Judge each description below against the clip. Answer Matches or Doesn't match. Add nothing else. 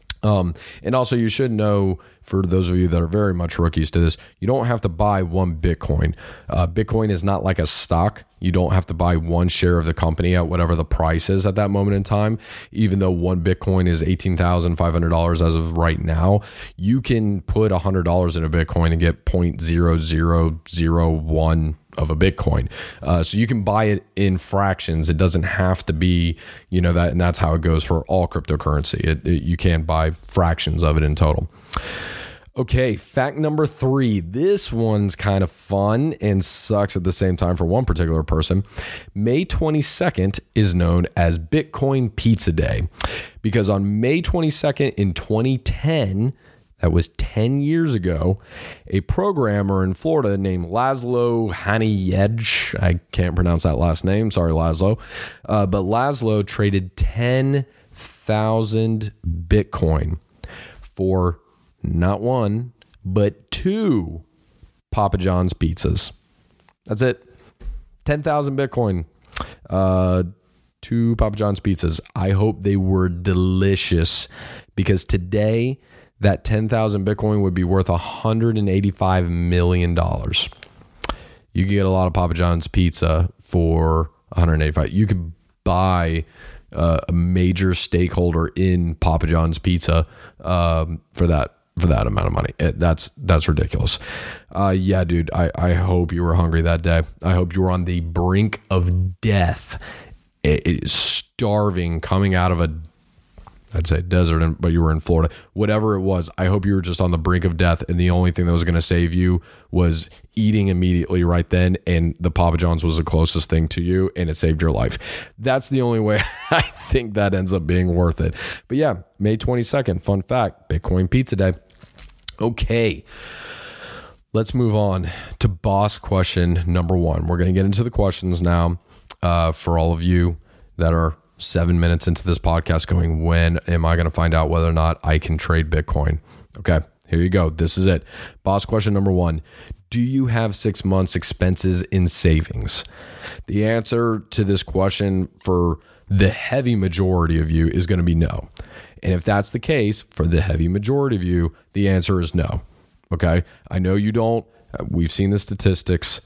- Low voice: Matches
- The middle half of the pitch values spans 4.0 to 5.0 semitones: Doesn't match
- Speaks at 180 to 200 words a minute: Doesn't match